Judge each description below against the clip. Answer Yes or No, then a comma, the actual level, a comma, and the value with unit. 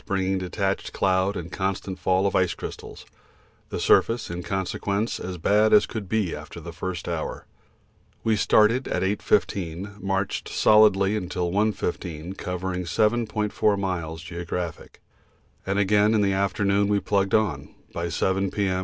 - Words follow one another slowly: No, average, 145 wpm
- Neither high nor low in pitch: No, very low, 95 Hz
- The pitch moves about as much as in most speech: No, narrow, 2.2 semitones